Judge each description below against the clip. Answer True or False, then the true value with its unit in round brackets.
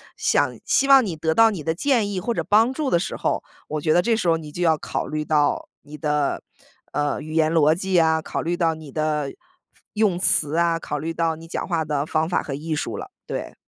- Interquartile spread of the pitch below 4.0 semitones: True (2.9 semitones)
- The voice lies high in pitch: False (165 Hz)